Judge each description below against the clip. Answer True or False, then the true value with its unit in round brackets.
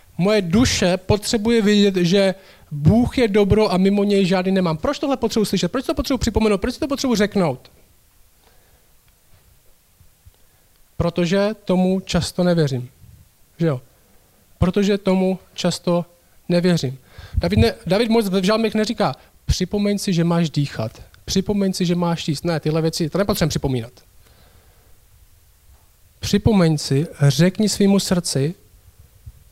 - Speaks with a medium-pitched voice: True (175 Hz)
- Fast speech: False (125 wpm)